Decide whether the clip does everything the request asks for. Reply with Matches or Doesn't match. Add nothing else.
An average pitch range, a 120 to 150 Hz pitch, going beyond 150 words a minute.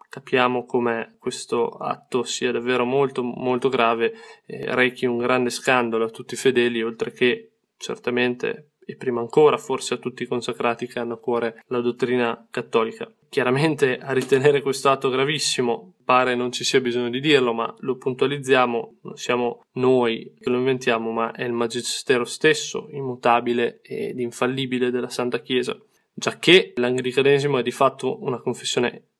Doesn't match